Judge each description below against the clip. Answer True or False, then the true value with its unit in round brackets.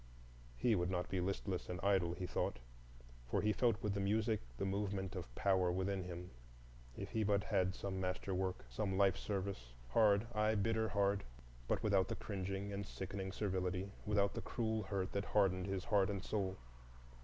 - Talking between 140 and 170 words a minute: False (185 wpm)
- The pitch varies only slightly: True (1.7 semitones)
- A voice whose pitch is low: True (100 Hz)